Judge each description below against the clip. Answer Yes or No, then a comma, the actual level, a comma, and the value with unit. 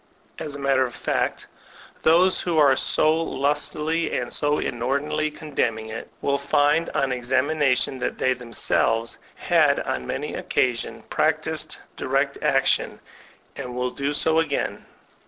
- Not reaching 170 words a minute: Yes, slow, 135 wpm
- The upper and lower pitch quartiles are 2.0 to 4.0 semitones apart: Yes, average, 3.4 semitones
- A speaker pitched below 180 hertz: Yes, medium, 140 Hz